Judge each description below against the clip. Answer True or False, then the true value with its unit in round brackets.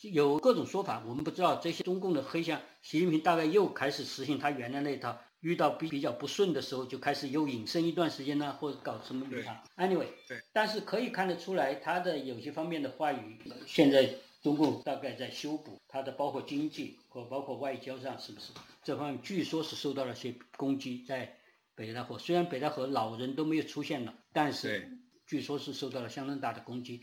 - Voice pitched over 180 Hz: False (145 Hz)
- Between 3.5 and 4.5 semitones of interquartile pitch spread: True (4.0 semitones)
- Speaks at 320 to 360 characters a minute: True (335 characters per minute)